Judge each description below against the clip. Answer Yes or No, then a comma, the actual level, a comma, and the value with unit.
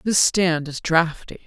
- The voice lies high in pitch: No, medium, 170 Hz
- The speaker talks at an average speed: Yes, average, 165 wpm